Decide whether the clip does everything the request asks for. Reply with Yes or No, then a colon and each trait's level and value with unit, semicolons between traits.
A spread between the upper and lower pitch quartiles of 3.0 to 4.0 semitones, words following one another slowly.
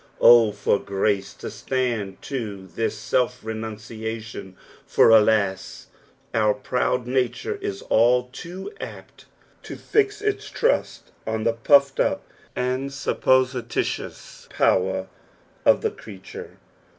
Yes: average, 3.5 semitones; slow, 115 wpm